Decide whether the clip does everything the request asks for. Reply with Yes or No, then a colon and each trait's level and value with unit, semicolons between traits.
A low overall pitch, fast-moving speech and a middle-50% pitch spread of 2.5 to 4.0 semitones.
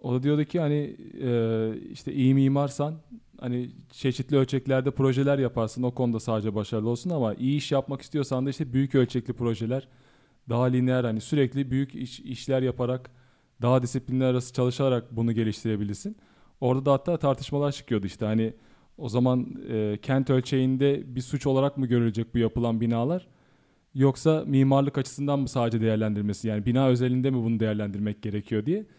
Yes: low, 130 Hz; fast, 160 wpm; average, 2.8 semitones